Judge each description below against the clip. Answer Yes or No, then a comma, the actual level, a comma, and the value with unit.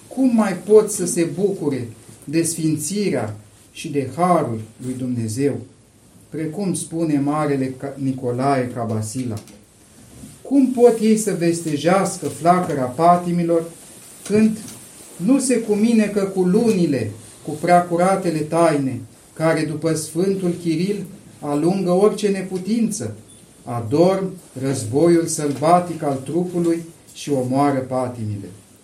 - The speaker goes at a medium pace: No, slow, 100 wpm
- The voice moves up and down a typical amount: No, wide, 6.1 semitones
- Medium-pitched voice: Yes, medium, 160 Hz